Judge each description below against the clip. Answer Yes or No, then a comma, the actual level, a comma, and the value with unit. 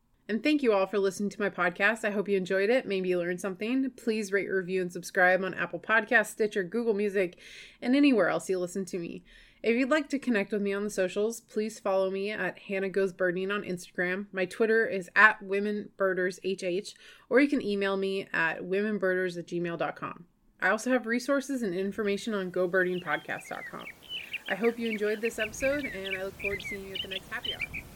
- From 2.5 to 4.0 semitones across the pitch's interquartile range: Yes, average, 2.8 semitones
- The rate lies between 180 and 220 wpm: Yes, fast, 205 wpm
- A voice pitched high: Yes, high, 200 Hz